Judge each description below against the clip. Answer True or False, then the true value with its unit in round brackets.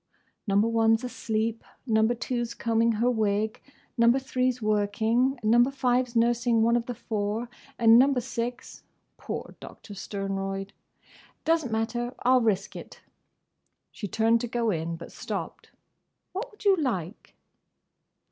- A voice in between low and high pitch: False (230 Hz)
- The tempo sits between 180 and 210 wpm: False (140 wpm)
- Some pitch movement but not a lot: False (2.2 semitones)